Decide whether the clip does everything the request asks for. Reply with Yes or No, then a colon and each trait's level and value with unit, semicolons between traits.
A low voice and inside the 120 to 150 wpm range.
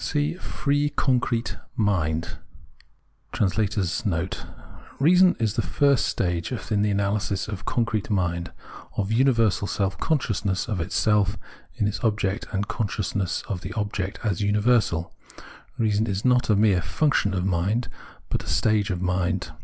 Yes: low, 105 Hz; average, 145 wpm